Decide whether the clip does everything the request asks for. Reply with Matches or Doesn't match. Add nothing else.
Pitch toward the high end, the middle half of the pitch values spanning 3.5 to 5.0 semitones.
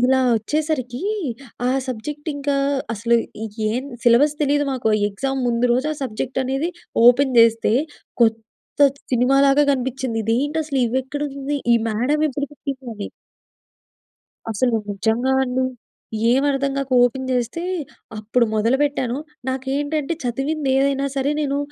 Doesn't match